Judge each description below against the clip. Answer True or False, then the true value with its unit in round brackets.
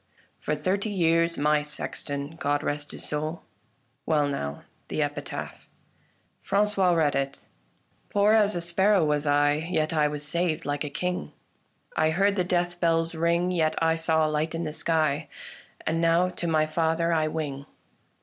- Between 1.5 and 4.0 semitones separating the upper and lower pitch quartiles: True (2.7 semitones)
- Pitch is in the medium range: True (160 Hz)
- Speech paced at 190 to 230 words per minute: False (170 wpm)